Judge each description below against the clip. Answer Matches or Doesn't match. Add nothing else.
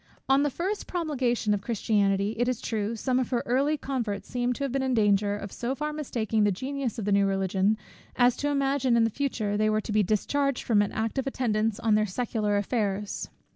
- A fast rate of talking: Matches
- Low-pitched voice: Doesn't match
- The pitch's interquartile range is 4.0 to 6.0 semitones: Matches